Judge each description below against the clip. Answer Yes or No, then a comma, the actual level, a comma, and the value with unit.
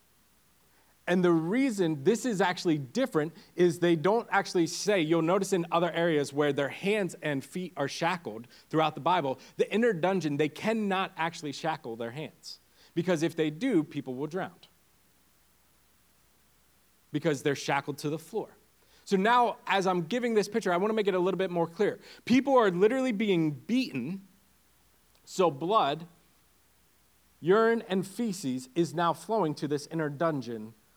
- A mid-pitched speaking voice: Yes, medium, 170 Hz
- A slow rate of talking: No, average, 160 wpm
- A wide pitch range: No, average, 4.7 semitones